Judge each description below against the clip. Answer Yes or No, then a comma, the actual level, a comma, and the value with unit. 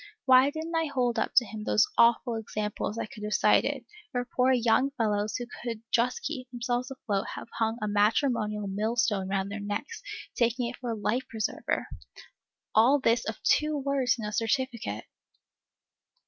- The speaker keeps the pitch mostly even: No, average, 3.2 semitones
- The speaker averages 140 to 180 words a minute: Yes, average, 175 wpm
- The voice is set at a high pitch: Yes, high, 235 Hz